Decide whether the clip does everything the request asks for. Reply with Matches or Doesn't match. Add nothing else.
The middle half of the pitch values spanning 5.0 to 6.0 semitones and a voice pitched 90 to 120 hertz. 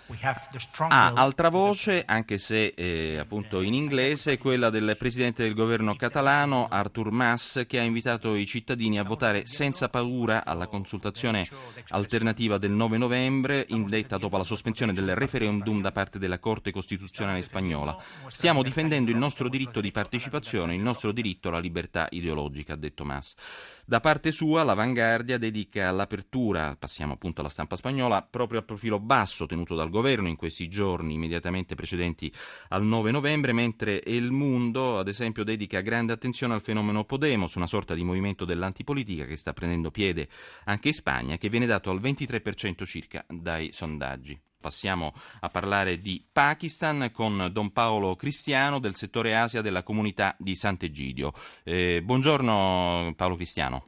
Matches